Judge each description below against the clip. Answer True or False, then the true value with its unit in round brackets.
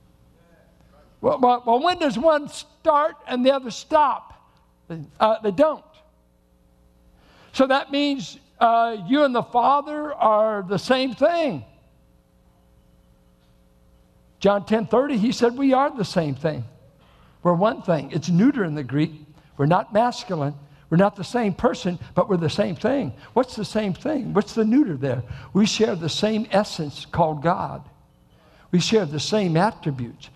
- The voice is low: False (195 Hz)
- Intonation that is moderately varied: False (8.7 semitones)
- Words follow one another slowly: False (150 wpm)